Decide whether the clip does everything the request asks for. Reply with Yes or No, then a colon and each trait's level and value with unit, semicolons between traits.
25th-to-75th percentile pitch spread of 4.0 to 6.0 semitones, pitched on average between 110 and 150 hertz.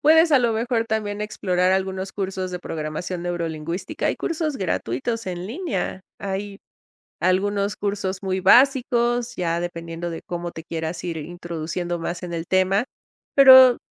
No: average, 4.7 semitones; high, 190 Hz